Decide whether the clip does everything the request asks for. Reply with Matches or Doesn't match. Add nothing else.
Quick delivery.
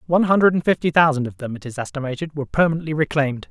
Matches